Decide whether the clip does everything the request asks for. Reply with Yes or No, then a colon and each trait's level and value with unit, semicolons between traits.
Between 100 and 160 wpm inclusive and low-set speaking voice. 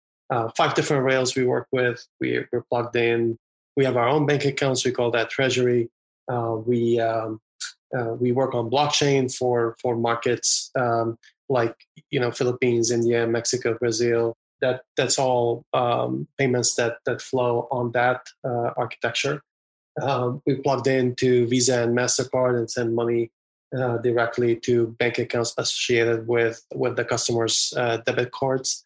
Yes: average, 155 wpm; low, 120 Hz